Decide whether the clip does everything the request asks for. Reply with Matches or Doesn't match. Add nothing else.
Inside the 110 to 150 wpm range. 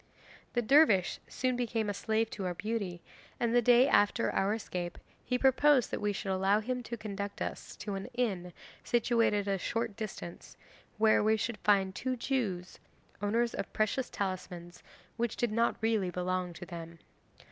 Doesn't match